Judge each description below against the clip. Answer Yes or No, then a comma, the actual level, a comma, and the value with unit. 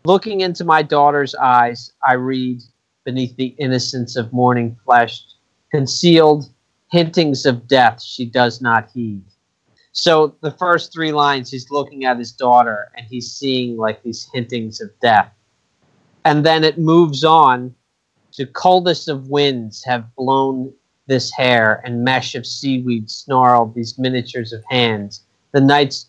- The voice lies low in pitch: Yes, low, 130 Hz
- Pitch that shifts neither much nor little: Yes, average, 3.2 semitones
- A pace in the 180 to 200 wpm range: No, average, 145 wpm